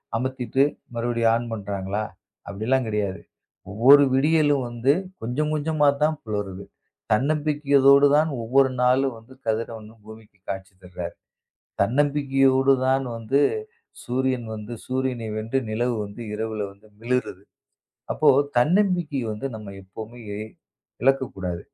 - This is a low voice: Yes, low, 120 Hz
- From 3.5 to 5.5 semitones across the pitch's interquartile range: Yes, average, 4.1 semitones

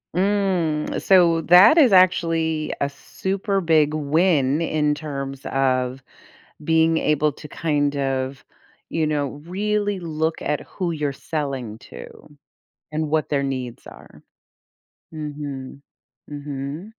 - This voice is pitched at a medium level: Yes, medium, 155 Hz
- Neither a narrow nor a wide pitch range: Yes, average, 3.2 semitones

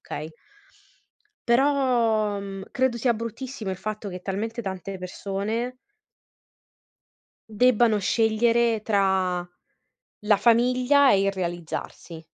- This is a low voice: No, high, 215 Hz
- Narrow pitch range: No, average, 3.5 semitones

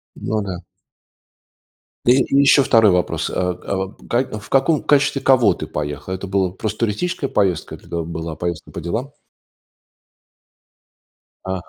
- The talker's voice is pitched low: Yes, low, 100 Hz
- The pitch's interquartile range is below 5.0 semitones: No, wide, 6.4 semitones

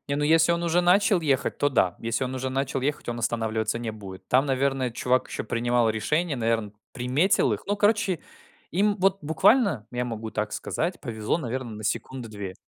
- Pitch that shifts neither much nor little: No, wide, 6.3 semitones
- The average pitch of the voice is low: Yes, low, 130 Hz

